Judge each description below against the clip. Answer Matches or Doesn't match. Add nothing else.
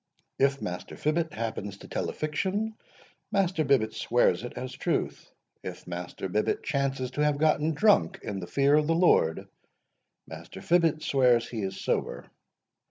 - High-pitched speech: Doesn't match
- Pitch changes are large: Matches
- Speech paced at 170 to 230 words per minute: Doesn't match